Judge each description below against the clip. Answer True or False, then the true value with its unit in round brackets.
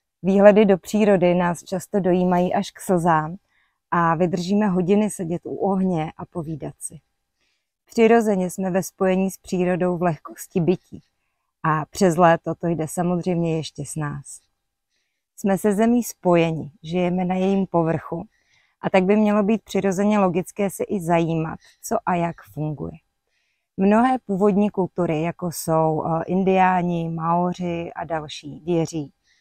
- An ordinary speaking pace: True (140 wpm)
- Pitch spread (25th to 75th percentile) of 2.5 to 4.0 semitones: True (2.9 semitones)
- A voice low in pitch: False (180 Hz)